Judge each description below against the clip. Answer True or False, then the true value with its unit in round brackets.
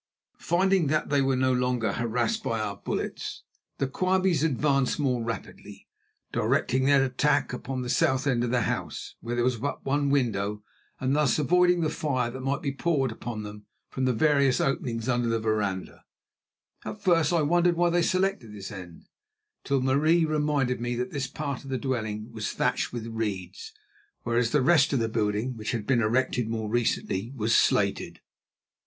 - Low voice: True (130 Hz)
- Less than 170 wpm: False (180 wpm)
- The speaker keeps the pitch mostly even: False (4.3 semitones)